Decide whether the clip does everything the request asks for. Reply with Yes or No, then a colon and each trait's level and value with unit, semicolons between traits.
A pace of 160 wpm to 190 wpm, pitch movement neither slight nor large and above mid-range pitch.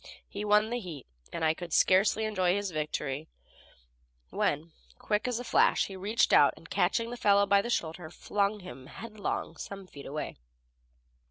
Yes: average, 170 wpm; average, 4.8 semitones; high, 200 Hz